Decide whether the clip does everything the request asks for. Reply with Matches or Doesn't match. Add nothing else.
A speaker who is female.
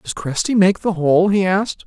Doesn't match